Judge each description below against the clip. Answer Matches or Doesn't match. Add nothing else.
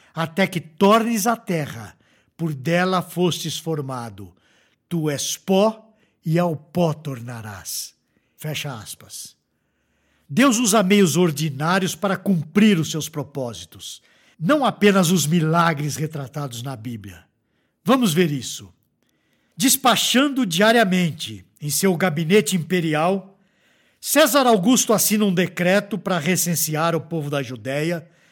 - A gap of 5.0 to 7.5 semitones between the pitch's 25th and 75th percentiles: Matches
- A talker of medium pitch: Matches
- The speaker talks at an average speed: Doesn't match